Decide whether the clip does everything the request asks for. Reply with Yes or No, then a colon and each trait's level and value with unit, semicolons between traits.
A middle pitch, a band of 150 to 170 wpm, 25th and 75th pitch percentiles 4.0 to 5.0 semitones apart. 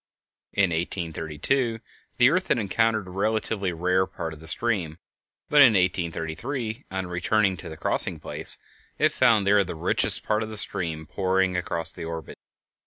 No: very low, 95 Hz; average, 165 wpm; average, 4.7 semitones